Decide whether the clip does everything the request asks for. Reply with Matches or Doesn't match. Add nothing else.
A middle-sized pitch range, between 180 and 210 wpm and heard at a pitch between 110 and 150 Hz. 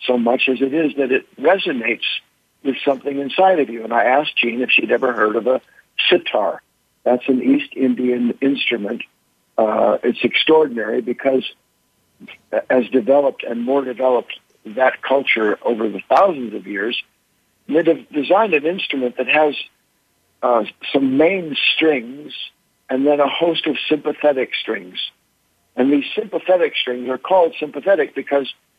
Doesn't match